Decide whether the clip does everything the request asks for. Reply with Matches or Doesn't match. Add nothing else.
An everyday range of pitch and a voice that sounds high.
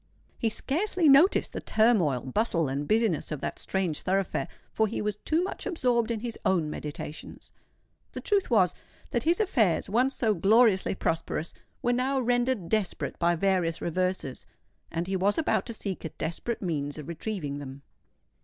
Doesn't match